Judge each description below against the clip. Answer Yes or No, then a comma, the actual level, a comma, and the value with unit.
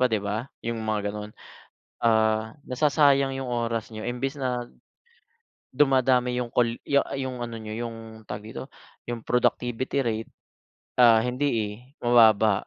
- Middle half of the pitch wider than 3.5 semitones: No, narrow, 2.4 semitones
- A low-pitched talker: Yes, low, 120 Hz